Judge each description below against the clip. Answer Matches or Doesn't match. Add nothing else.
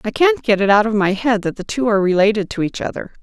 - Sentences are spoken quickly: Matches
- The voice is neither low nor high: Doesn't match